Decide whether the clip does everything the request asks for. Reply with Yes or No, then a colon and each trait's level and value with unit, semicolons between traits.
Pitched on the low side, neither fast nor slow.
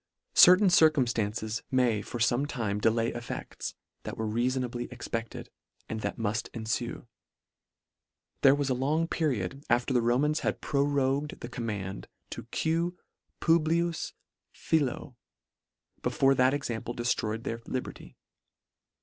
No: low, 125 Hz; slow, 130 wpm